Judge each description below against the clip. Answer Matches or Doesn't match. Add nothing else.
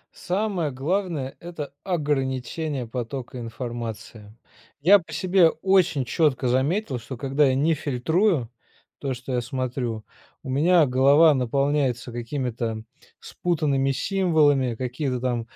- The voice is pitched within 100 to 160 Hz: Matches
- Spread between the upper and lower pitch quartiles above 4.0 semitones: Matches